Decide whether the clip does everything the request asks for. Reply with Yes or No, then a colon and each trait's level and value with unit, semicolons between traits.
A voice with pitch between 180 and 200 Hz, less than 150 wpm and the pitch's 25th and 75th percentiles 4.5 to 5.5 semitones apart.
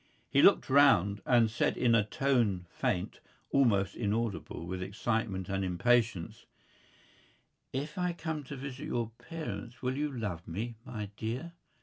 No: low, 115 Hz; average, 140 wpm; average, 5.0 semitones